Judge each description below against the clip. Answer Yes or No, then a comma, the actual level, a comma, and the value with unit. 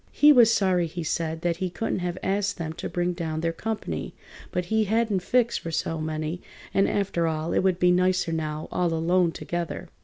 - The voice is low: No, medium, 175 Hz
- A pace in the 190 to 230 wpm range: Yes, fast, 205 wpm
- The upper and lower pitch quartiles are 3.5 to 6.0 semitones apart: No, average, 2.9 semitones